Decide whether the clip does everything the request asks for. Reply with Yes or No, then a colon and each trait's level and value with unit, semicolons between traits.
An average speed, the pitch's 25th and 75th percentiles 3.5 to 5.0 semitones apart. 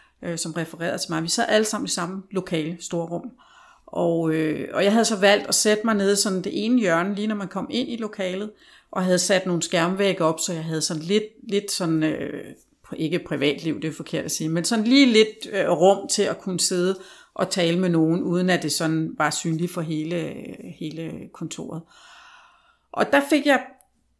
Yes: average, 210 wpm; average, 4.5 semitones